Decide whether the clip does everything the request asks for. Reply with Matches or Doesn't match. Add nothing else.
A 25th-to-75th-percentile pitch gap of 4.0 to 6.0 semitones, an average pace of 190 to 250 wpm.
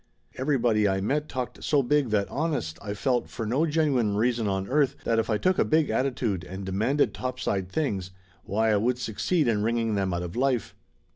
Matches